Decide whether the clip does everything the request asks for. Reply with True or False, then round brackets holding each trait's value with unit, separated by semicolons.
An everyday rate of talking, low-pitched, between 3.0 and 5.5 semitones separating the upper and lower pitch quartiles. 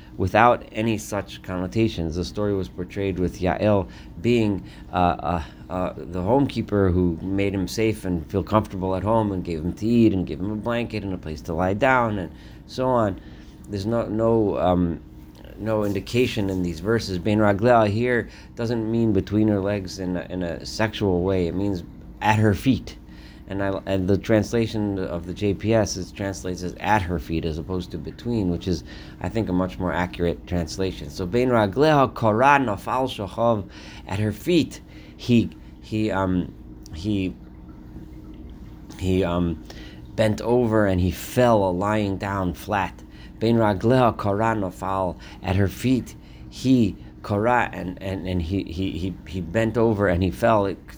True (155 wpm; 95 Hz; 3.9 semitones)